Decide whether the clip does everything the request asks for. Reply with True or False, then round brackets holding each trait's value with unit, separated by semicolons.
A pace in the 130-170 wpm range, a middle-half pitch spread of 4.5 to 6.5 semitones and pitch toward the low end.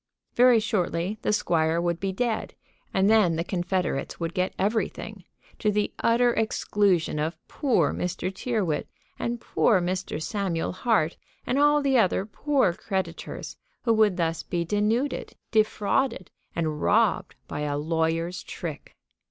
False (140 wpm; 4.8 semitones; 190 Hz)